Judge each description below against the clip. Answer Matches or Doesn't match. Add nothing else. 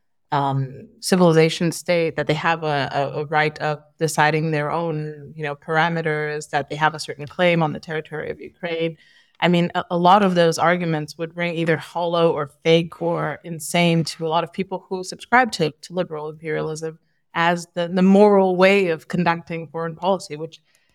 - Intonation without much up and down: Matches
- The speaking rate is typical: Matches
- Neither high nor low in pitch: Matches